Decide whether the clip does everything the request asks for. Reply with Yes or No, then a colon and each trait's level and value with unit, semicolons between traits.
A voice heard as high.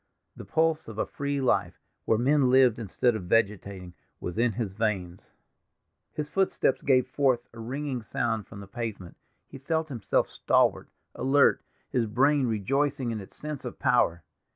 No: low, 120 Hz